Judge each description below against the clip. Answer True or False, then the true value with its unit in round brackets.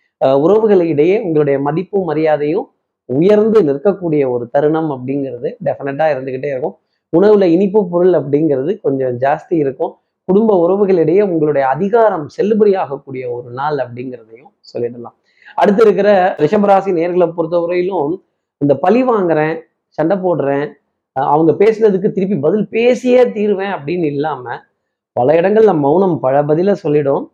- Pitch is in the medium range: True (170 Hz)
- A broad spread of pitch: True (6.0 semitones)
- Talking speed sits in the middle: True (115 wpm)